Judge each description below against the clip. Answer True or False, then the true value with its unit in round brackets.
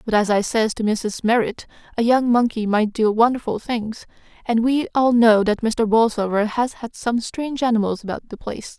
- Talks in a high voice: True (225 Hz)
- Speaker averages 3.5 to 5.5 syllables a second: True (5.1 syllables/s)